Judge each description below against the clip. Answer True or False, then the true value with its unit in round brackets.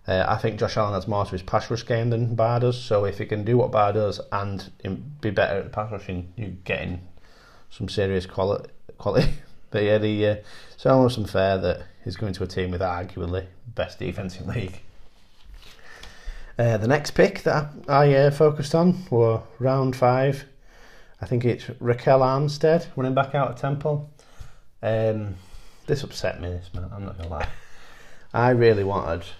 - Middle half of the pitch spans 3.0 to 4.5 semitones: False (5.0 semitones)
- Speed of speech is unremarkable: True (185 wpm)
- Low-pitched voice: True (110 Hz)